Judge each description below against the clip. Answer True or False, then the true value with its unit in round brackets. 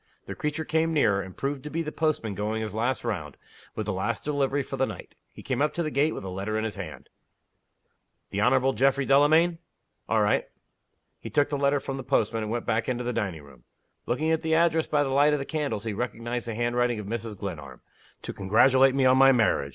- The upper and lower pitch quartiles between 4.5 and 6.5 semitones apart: True (5.1 semitones)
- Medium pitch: False (130 Hz)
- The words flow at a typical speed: False (230 wpm)